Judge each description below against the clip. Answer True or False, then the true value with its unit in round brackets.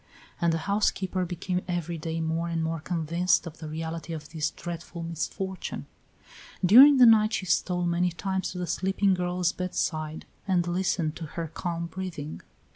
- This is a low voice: False (175 Hz)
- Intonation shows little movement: True (2.1 semitones)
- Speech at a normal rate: True (165 wpm)